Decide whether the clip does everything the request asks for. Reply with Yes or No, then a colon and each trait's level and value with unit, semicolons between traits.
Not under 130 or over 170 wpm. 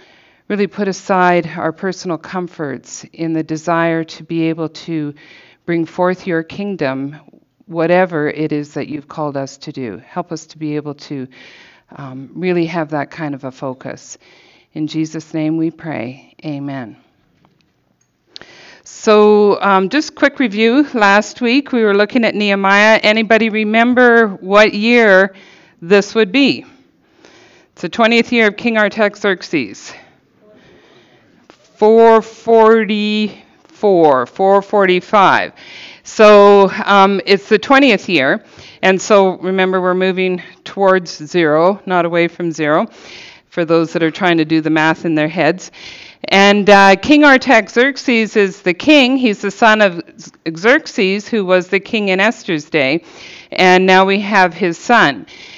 Yes: average, 140 wpm